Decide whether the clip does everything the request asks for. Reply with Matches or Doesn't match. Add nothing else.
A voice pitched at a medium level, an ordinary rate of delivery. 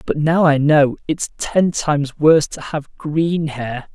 Matches